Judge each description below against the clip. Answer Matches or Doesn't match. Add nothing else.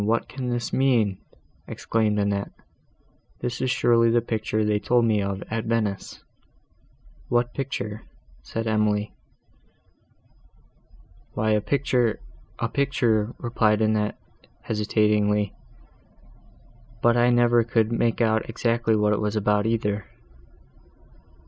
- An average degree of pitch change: Doesn't match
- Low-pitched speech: Matches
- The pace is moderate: Doesn't match